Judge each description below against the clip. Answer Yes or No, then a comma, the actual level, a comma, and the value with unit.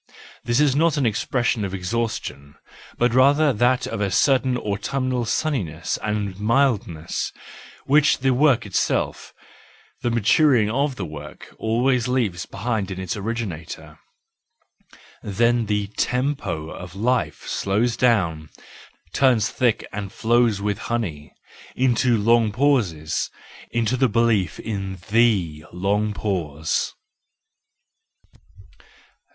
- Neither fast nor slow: No, slow, 105 wpm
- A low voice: Yes, low, 110 Hz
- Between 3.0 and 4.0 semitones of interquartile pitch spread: No, average, 4.5 semitones